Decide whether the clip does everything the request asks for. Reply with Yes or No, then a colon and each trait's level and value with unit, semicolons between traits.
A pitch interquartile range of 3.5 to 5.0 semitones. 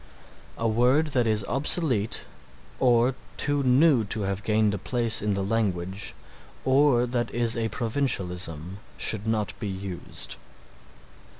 Yes: average, 4.0 semitones